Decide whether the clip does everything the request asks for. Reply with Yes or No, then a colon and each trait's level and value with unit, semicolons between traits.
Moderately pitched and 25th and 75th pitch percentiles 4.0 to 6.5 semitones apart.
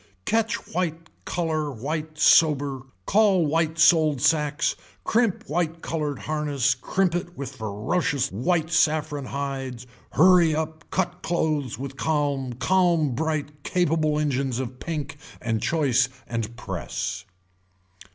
No: medium, 150 Hz; average, 3.2 semitones